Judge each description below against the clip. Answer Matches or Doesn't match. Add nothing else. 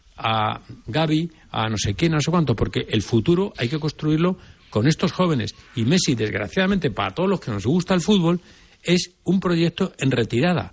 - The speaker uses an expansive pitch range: Matches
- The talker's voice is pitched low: Doesn't match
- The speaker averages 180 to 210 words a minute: Matches